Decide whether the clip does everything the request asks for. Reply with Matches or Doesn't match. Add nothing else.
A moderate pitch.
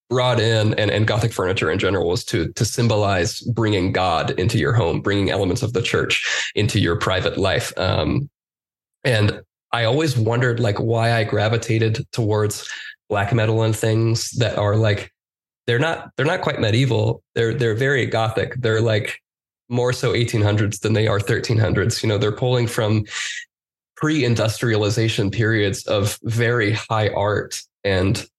Doesn't match